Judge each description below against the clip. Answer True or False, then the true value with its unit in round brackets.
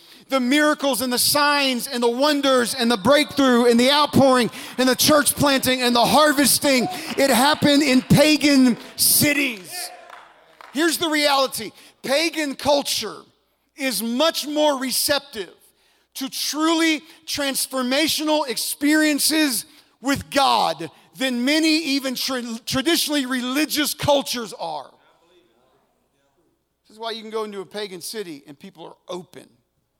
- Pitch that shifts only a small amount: False (3.5 semitones)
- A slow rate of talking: True (125 wpm)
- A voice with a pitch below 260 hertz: False (270 Hz)